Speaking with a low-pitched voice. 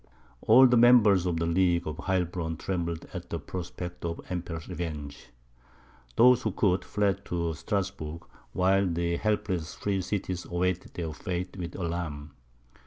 Yes: very low, 90 Hz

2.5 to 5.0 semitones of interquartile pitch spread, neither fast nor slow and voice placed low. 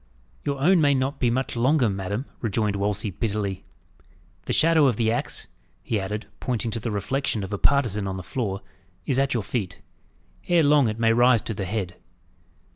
Yes: average, 4.6 semitones; average, 190 wpm; low, 115 Hz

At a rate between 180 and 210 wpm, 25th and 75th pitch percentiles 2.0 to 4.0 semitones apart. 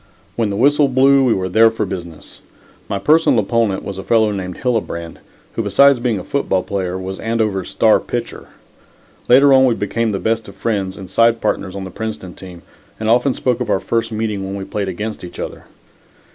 Yes: average, 200 wpm; average, 3.5 semitones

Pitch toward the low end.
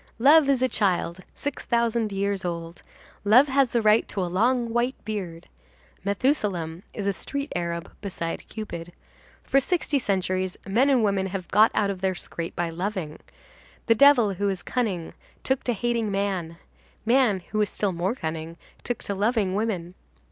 No: high, 200 Hz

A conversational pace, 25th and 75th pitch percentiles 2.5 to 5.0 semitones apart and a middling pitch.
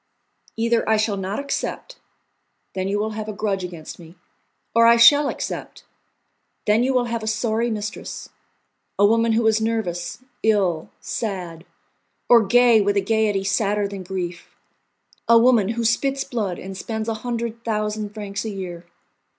No: average, 160 wpm; average, 2.9 semitones; high, 215 Hz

